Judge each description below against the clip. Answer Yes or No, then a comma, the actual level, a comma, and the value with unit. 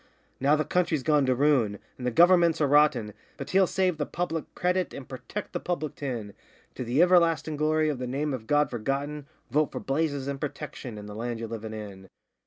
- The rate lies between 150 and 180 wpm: No, fast, 205 wpm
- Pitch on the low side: No, medium, 145 Hz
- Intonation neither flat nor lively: Yes, average, 4.2 semitones